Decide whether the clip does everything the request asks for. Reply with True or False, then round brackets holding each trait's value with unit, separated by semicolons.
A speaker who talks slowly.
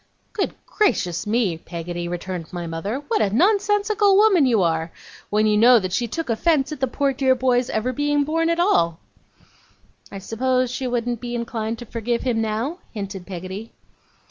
False (175 wpm)